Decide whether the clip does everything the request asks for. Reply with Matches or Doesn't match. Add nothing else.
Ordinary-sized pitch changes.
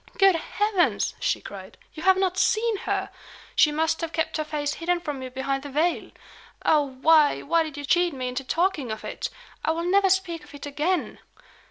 Matches